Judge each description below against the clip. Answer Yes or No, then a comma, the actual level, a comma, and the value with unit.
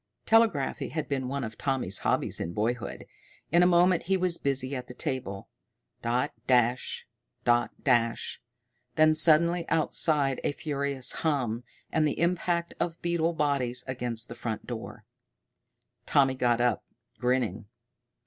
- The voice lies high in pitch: No, low, 135 Hz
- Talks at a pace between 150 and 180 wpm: No, average, 140 wpm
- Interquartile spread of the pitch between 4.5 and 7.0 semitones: Yes, average, 4.8 semitones